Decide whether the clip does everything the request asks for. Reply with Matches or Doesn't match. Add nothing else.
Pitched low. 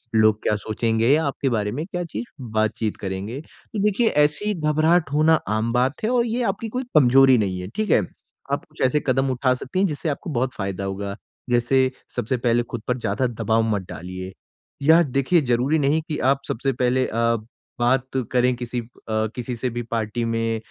Matches